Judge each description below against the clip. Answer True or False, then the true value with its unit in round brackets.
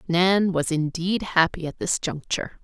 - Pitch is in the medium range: True (170 Hz)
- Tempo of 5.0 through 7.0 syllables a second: False (4.5 syllables/s)